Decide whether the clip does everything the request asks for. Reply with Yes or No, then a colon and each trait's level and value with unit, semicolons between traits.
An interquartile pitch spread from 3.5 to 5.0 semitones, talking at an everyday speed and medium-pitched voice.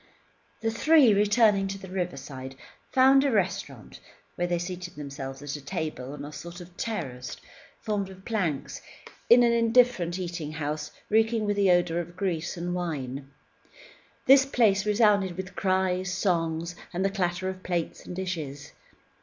Yes: average, 4.1 semitones; average, 155 wpm; medium, 180 Hz